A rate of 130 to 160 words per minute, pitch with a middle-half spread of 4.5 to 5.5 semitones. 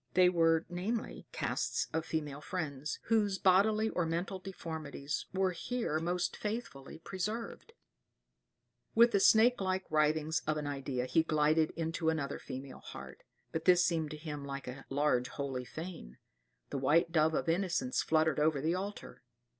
No: average, 155 wpm; average, 3.9 semitones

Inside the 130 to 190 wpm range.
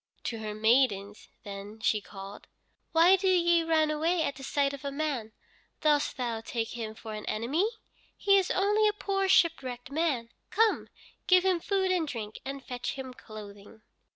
Yes: average, 175 wpm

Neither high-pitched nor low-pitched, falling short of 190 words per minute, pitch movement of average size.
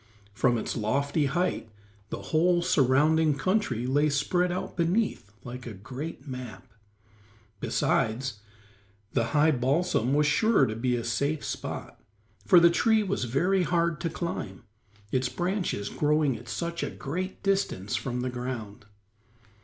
No: medium, 145 Hz; average, 140 wpm; wide, 5.8 semitones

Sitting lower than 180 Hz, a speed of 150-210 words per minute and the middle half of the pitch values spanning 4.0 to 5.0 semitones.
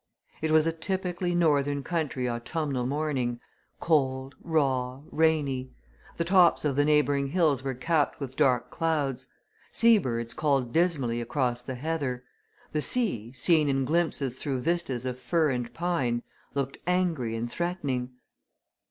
No: medium, 140 Hz; average, 140 wpm; average, 4.3 semitones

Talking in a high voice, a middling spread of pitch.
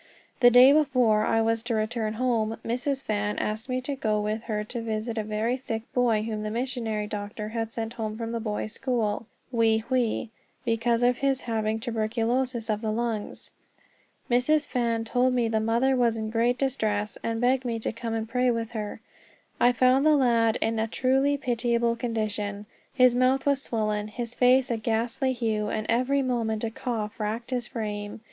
No: high, 230 Hz; narrow, 2.3 semitones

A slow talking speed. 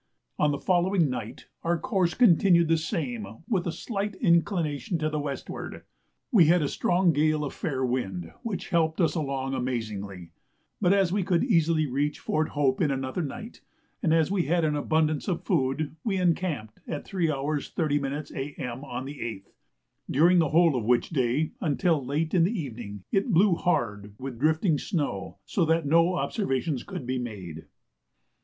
No: average, 170 wpm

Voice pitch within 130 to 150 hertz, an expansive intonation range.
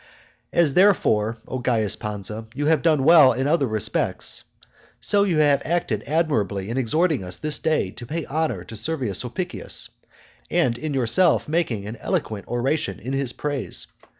Yes: low, 135 Hz; wide, 6.2 semitones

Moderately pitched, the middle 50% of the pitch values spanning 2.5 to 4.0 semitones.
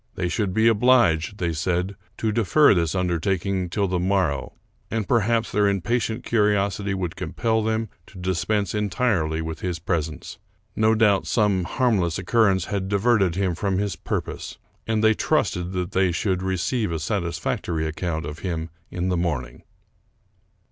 No: very low, 95 Hz; average, 3.7 semitones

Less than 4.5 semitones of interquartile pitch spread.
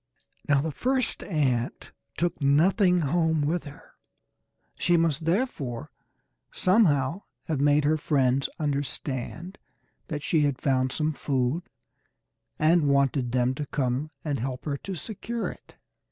Yes: average, 3.8 semitones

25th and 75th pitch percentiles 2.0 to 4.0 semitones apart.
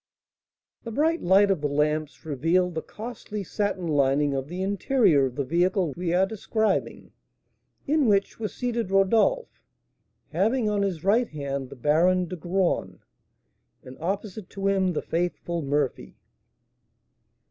No: average, 5.2 semitones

